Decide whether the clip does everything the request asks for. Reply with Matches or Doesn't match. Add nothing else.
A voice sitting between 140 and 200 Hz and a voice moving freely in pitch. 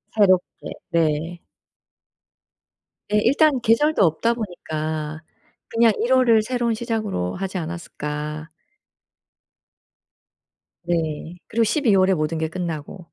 Matches